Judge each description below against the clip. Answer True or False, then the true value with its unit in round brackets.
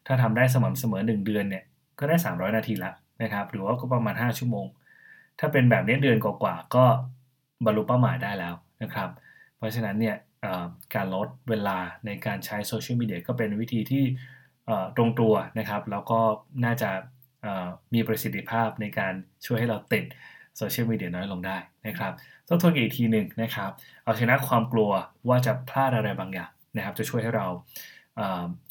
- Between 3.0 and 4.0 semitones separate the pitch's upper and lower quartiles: True (3.5 semitones)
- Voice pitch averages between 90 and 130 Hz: True (110 Hz)